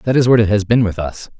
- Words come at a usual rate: No, fast, 345 wpm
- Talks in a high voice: No, low, 105 Hz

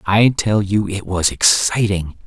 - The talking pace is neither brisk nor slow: Yes, average, 160 wpm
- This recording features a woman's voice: No, male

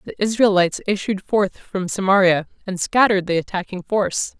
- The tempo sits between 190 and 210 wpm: No, average, 150 wpm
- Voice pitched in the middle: No, high, 195 Hz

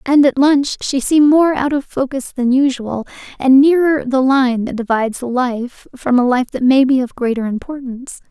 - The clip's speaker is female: Yes, female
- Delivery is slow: No, average, 195 wpm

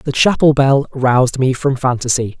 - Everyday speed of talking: Yes, average, 175 wpm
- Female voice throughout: No, male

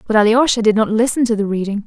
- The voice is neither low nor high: No, high, 220 Hz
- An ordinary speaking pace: No, fast, 255 wpm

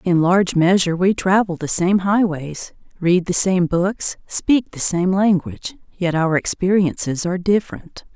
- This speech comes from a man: No, female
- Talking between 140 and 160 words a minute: Yes, average, 155 wpm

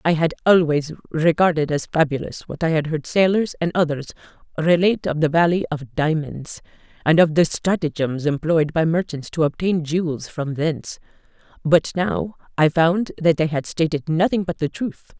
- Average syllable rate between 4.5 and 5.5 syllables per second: Yes, 5.0 syllables/s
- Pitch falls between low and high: Yes, medium, 160 Hz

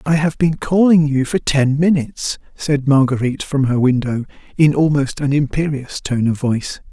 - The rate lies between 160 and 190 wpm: Yes, average, 175 wpm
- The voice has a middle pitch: Yes, medium, 145 Hz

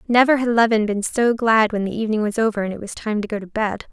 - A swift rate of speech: Yes, fast, 290 wpm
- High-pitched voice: Yes, high, 215 Hz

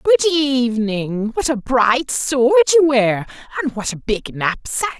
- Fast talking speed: No, average, 155 wpm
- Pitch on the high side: Yes, very high, 260 Hz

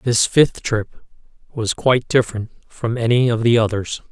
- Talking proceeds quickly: No, average, 160 wpm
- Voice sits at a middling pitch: No, low, 115 Hz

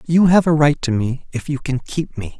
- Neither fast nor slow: No, fast, 275 wpm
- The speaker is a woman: No, male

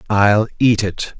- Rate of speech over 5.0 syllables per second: No, 3.5 syllables/s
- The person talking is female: No, male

